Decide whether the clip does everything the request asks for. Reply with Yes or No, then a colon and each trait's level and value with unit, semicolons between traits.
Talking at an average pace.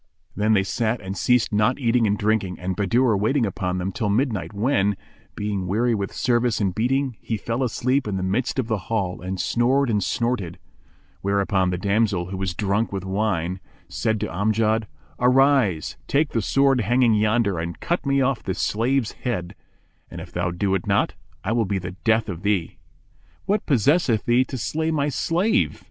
Yes: average, 185 wpm